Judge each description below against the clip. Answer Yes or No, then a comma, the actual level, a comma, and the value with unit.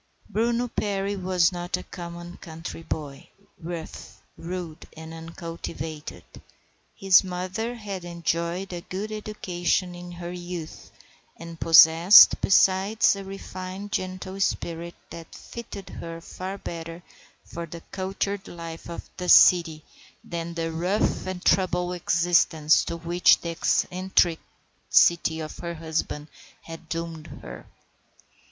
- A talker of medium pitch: Yes, medium, 175 Hz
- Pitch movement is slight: Yes, narrow, 2.1 semitones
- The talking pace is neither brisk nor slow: No, slow, 120 wpm